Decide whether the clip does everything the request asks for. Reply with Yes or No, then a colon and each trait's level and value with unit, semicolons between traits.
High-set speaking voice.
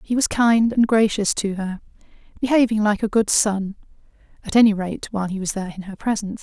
Yes: high, 210 Hz